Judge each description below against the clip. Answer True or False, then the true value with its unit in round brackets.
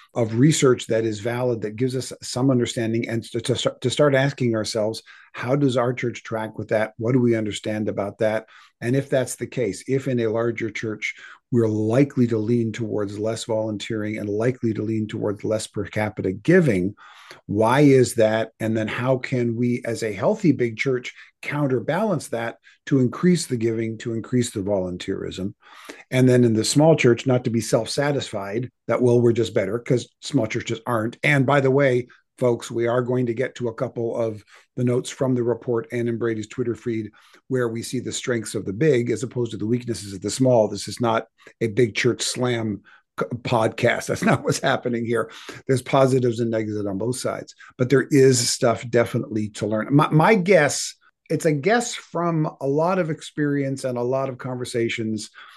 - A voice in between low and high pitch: False (120 Hz)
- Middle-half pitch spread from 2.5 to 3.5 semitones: True (2.8 semitones)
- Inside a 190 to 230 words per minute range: True (200 wpm)